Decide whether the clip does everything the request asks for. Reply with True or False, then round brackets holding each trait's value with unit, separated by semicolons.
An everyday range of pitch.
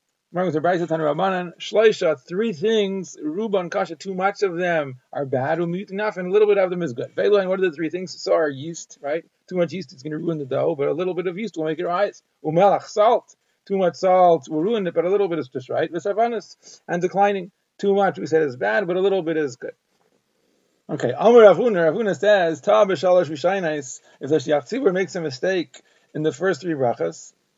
True (3.7 semitones)